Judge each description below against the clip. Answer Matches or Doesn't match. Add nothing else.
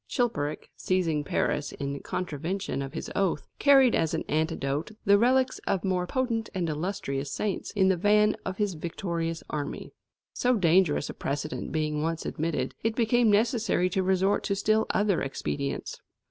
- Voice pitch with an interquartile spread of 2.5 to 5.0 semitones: Doesn't match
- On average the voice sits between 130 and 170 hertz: Doesn't match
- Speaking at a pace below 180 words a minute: Matches